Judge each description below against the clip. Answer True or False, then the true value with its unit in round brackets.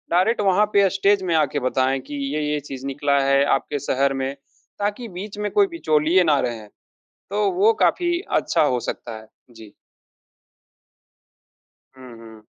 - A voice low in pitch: False (150 Hz)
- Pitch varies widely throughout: True (7.2 semitones)